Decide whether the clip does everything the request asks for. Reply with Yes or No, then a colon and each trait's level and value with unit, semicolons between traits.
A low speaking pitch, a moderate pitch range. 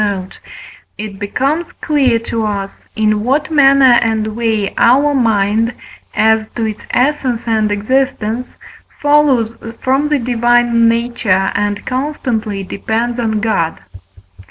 No: high, 230 Hz; average, 3.4 semitones